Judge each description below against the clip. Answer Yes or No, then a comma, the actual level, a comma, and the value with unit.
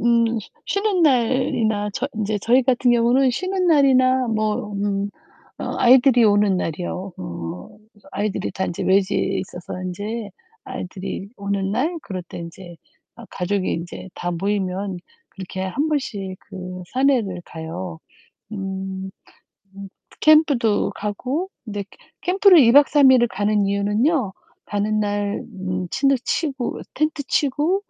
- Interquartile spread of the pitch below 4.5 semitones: No, wide, 5.4 semitones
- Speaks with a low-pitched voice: No, high, 205 Hz